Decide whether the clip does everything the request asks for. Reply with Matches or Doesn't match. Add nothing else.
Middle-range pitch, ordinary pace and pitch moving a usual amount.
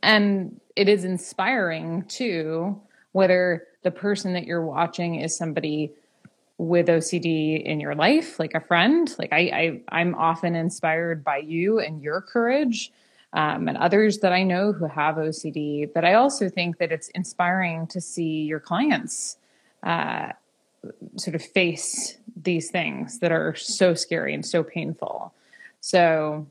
Matches